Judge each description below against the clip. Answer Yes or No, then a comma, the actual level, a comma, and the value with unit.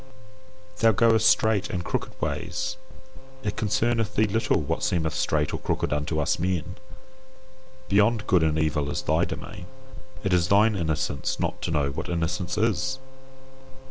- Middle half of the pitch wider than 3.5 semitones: Yes, average, 5.3 semitones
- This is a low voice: Yes, very low, 90 Hz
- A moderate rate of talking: Yes, average, 150 wpm